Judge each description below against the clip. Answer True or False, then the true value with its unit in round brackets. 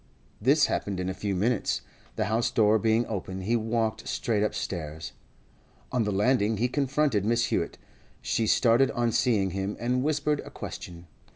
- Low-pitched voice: True (110 Hz)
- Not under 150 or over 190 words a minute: True (165 wpm)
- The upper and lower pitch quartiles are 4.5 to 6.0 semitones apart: False (3.6 semitones)